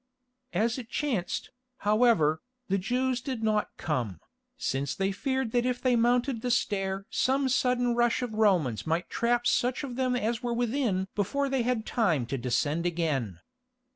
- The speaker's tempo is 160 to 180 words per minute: Yes, average, 165 wpm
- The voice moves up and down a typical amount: No, wide, 5.8 semitones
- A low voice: No, high, 230 Hz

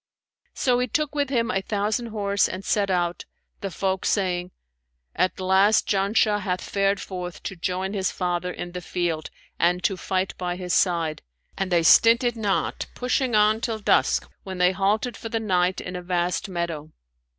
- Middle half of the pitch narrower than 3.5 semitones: Yes, average, 3.0 semitones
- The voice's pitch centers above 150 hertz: Yes, high, 190 Hz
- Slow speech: No, average, 175 wpm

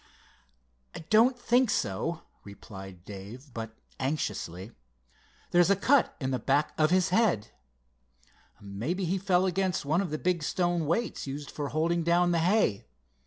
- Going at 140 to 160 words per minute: Yes, average, 150 wpm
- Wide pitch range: Yes, wide, 7.1 semitones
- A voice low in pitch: No, medium, 165 Hz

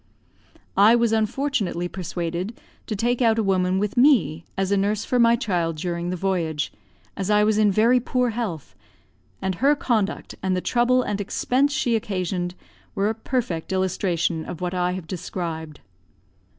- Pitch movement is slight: No, average, 4.7 semitones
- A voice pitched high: Yes, high, 195 Hz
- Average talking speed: Yes, average, 165 wpm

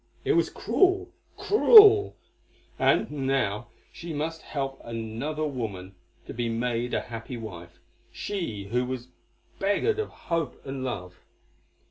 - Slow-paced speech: Yes, slow, 125 wpm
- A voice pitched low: Yes, low, 130 Hz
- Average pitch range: No, wide, 6.3 semitones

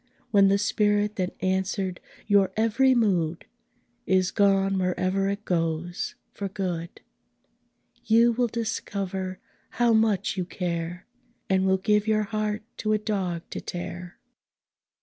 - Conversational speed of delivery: No, slow, 130 wpm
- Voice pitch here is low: No, high, 195 Hz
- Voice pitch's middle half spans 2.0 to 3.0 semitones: Yes, average, 2.7 semitones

